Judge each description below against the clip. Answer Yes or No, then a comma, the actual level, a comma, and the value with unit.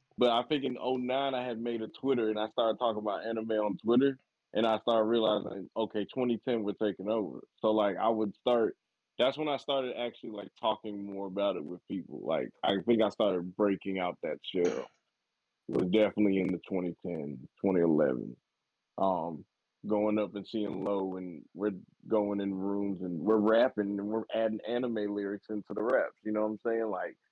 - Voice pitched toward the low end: Yes, low, 110 Hz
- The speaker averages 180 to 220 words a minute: Yes, average, 190 wpm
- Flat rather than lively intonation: Yes, narrow, 2.2 semitones